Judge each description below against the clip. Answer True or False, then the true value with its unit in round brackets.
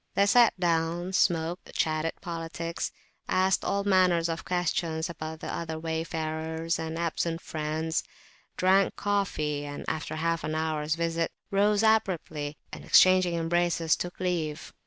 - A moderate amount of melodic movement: False (2.2 semitones)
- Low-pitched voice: False (165 Hz)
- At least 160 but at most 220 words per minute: False (135 wpm)